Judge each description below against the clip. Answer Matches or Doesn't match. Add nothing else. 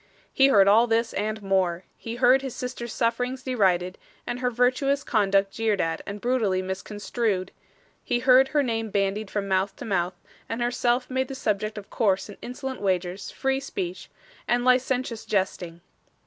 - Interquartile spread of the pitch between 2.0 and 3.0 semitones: Doesn't match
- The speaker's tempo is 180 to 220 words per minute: Doesn't match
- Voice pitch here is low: Doesn't match